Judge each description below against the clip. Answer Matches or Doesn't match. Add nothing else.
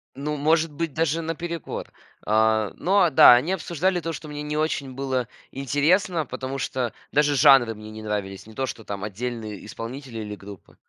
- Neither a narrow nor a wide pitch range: Doesn't match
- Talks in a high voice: Doesn't match